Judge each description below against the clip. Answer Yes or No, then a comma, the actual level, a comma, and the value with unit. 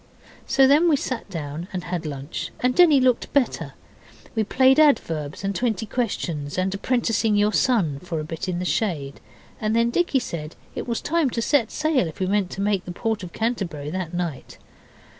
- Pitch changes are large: Yes, wide, 6.6 semitones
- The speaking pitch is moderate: No, high, 205 Hz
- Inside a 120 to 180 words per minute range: No, average, 195 wpm